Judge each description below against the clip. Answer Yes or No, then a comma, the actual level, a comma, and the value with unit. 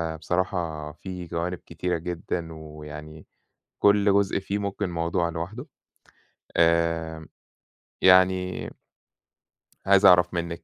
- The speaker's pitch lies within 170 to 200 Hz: No, very low, 85 Hz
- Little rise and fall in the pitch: Yes, narrow, 2.2 semitones